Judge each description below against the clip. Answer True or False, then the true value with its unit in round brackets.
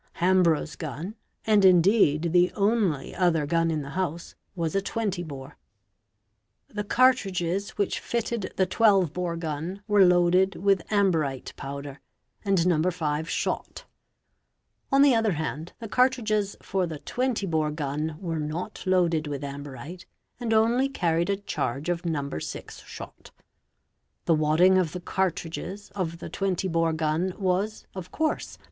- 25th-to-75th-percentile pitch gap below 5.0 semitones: True (4.0 semitones)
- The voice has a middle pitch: True (180 Hz)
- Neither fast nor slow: True (155 wpm)